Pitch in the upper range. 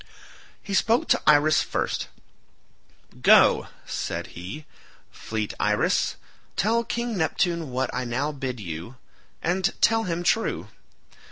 No: medium, 155 Hz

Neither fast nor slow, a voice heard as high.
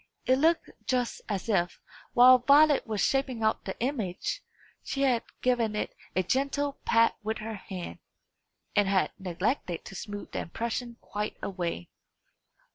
Yes: average, 145 wpm; high, 225 Hz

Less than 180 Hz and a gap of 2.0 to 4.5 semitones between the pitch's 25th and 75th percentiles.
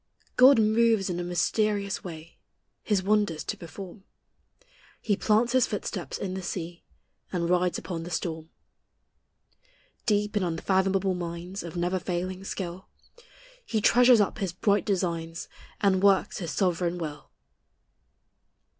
No: medium, 185 Hz; average, 3.0 semitones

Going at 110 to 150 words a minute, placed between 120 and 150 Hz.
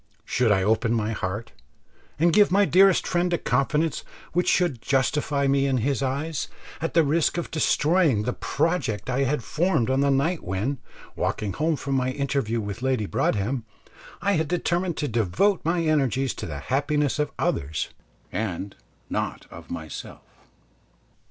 No: average, 160 wpm; medium, 140 Hz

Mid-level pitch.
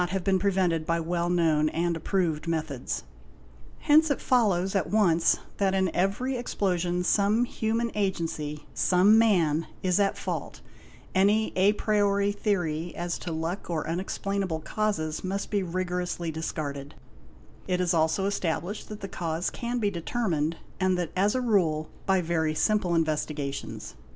Yes: medium, 180 Hz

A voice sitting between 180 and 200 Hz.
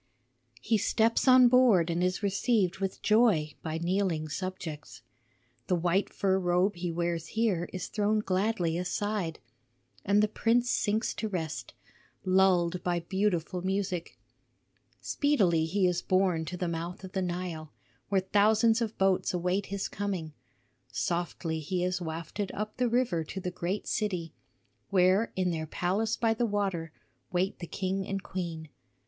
Yes: medium, 185 Hz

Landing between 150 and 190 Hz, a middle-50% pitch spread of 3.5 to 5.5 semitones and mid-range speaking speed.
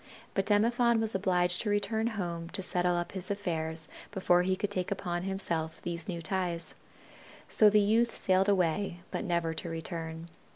No: medium, 185 Hz; average, 3.1 semitones; average, 170 wpm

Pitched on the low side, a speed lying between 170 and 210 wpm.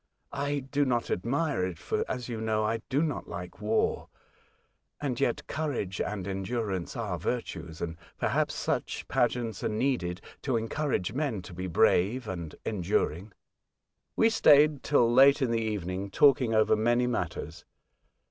No: low, 115 Hz; average, 150 wpm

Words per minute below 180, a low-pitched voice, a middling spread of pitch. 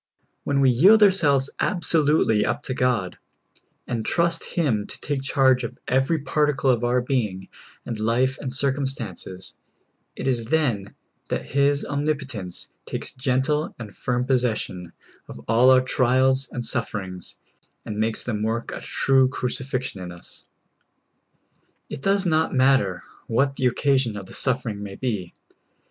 Yes: average, 150 wpm; low, 130 Hz; average, 3.8 semitones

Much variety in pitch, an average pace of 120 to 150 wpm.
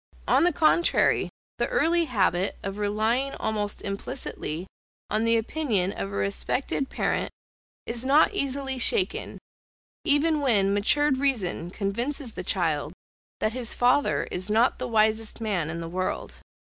Yes: wide, 5.8 semitones; average, 140 wpm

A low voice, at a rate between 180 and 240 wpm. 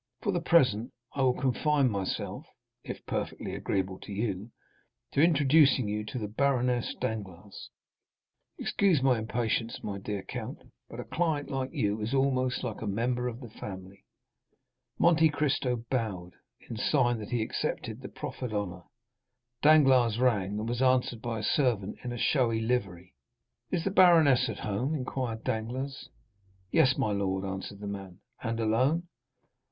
No: low, 120 Hz; average, 150 wpm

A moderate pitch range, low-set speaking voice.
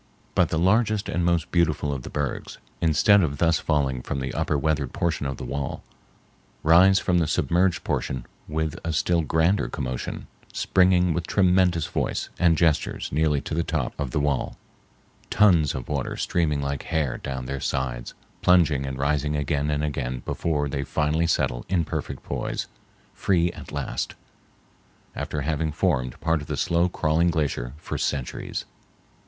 Yes: average, 3.4 semitones; very low, 75 Hz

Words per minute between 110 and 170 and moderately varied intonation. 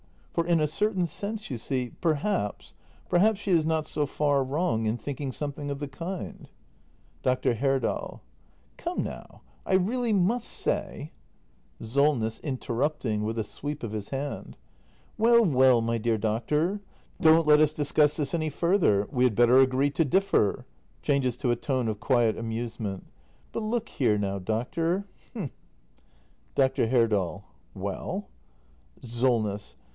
No: average, 150 wpm; wide, 5.9 semitones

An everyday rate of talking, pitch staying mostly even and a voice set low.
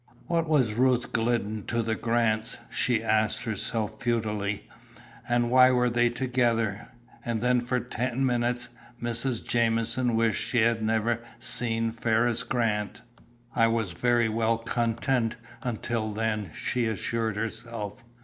No: slow, 130 wpm; narrow, 1.5 semitones; low, 115 Hz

